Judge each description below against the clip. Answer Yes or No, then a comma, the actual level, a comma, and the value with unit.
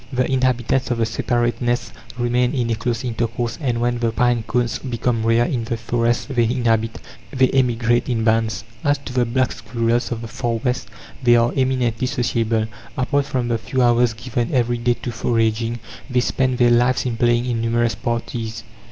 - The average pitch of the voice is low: Yes, low, 120 Hz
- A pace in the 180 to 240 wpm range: Yes, average, 185 wpm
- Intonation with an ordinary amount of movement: No, narrow, 1.4 semitones